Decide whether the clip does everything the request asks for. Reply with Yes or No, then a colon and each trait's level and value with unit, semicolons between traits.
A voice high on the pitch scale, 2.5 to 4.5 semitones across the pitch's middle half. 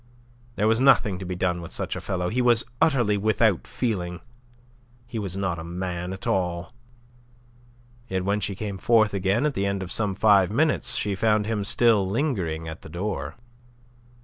No: low, 100 Hz; average, 3.4 semitones